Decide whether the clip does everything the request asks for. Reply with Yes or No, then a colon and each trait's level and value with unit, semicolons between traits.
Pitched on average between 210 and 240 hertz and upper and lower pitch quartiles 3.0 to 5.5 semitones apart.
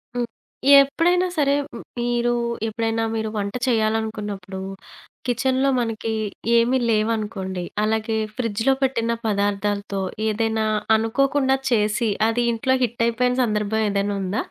No: high, 225 Hz; narrow, 2.4 semitones